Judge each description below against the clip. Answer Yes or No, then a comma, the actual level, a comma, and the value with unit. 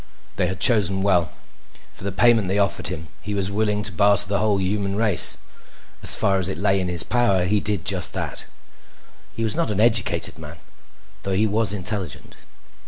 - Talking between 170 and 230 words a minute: Yes, average, 190 wpm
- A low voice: Yes, low, 100 Hz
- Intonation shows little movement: Yes, narrow, 2.2 semitones